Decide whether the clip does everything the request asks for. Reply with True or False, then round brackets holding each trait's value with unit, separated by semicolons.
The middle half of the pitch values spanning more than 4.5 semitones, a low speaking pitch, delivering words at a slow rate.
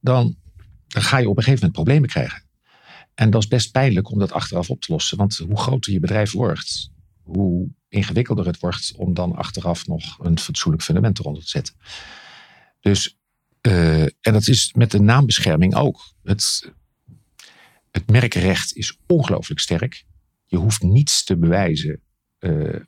False (5.3 semitones; 100 Hz; 165 wpm)